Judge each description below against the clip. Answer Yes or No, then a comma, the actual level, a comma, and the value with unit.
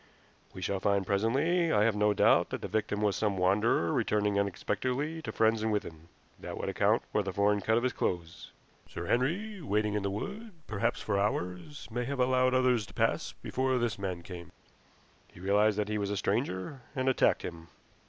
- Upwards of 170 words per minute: Yes, average, 195 wpm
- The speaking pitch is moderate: No, low, 105 Hz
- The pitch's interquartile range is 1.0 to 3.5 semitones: No, average, 4.5 semitones